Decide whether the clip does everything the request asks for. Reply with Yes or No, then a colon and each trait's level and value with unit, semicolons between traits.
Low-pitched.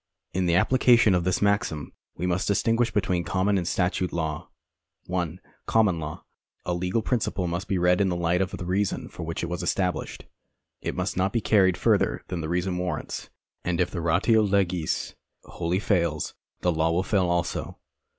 Yes: very low, 90 Hz